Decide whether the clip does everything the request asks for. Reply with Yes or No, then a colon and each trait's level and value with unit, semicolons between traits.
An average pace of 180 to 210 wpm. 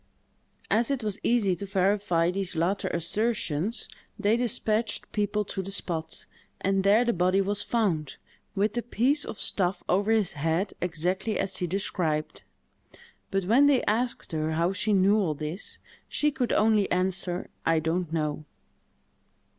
No: average, 155 wpm